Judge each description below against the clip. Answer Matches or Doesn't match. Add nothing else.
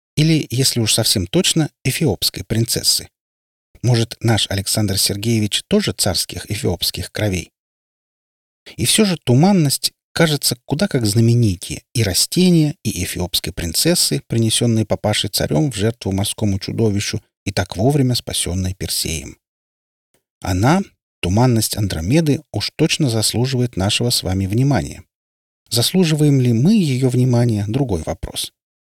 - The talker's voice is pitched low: Matches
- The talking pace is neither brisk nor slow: Matches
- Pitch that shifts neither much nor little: Doesn't match